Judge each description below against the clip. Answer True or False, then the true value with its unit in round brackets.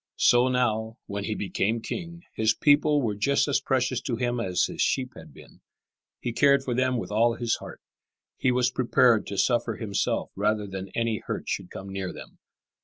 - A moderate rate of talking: True (190 wpm)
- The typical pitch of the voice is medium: False (115 Hz)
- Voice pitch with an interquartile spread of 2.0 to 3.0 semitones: False (3.4 semitones)